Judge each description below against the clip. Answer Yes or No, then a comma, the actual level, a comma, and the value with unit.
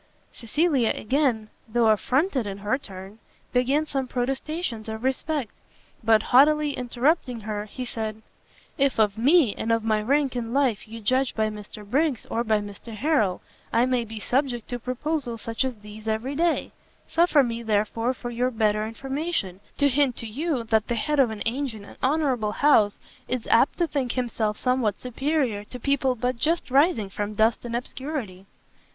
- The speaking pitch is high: Yes, high, 240 Hz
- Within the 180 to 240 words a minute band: No, average, 170 wpm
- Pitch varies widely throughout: No, average, 4.0 semitones